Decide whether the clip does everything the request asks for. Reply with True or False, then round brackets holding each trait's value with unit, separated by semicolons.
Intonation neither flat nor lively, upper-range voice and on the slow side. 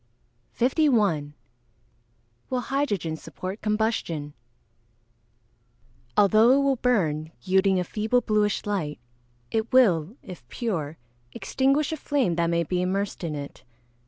False (6.6 semitones; 200 Hz; 115 wpm)